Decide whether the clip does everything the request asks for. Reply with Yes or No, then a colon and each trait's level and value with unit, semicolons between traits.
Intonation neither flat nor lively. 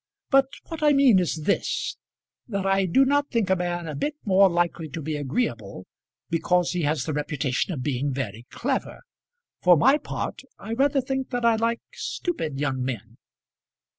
No: wide, 9.0 semitones